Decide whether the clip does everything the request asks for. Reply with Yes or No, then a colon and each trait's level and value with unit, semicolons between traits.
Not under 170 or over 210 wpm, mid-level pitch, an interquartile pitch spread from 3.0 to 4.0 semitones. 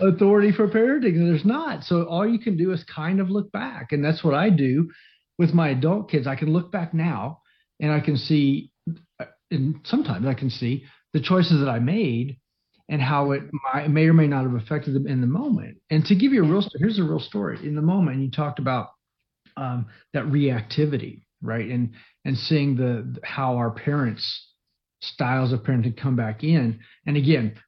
No: average, 200 wpm; medium, 150 Hz; average, 4.6 semitones